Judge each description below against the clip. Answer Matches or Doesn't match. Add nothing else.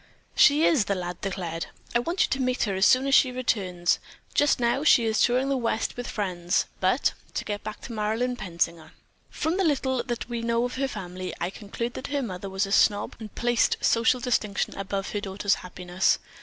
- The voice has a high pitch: Matches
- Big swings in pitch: Doesn't match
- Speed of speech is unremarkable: Doesn't match